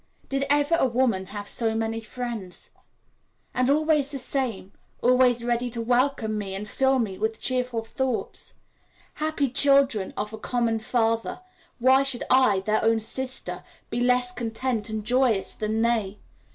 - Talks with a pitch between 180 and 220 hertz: No, high, 240 Hz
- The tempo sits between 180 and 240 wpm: No, average, 150 wpm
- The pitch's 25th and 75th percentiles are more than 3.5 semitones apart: No, average, 3.0 semitones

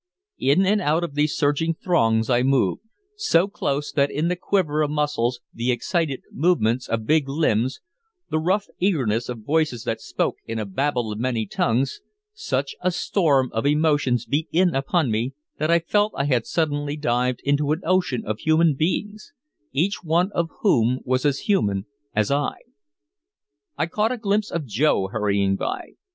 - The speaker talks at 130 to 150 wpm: No, average, 170 wpm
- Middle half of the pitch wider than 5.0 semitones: Yes, wide, 5.6 semitones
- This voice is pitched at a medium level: Yes, medium, 145 Hz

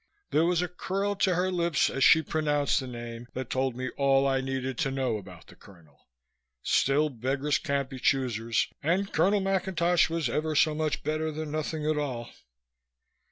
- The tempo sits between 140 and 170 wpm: No, average, 180 wpm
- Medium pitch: Yes, medium, 145 Hz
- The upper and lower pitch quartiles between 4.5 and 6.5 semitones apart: No, average, 3.8 semitones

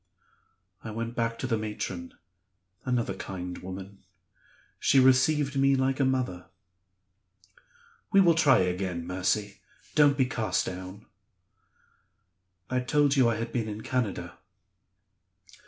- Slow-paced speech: Yes, slow, 120 wpm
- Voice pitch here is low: Yes, low, 115 Hz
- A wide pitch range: Yes, wide, 5.7 semitones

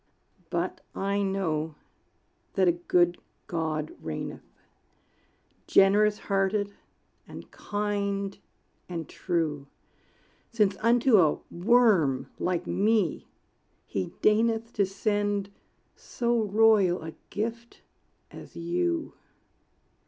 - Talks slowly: Yes, slow, 90 wpm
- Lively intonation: No, average, 4.1 semitones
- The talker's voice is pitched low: No, high, 195 Hz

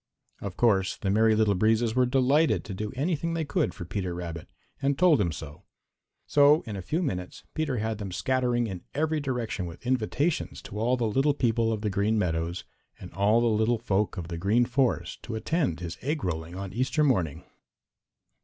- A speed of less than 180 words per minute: No, average, 195 wpm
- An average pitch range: No, wide, 5.7 semitones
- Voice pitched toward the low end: Yes, low, 110 Hz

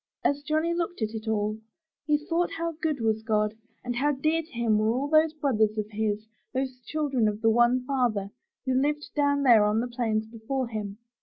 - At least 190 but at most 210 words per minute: Yes, fast, 205 wpm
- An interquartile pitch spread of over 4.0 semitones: Yes, average, 5.2 semitones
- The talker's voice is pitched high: Yes, high, 245 Hz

